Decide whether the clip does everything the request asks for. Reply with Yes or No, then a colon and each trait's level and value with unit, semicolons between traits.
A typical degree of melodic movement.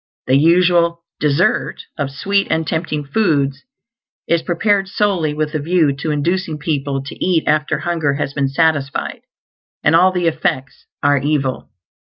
Yes: average, 3.3 semitones